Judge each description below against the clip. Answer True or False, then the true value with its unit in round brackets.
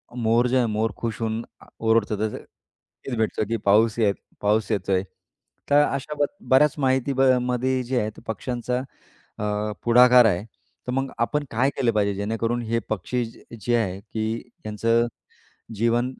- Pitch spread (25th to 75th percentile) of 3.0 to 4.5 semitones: False (2.6 semitones)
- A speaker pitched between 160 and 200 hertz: False (115 Hz)